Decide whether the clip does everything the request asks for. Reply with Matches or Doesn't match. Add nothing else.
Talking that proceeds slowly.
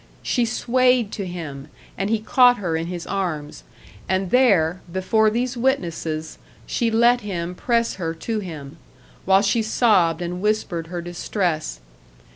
Doesn't match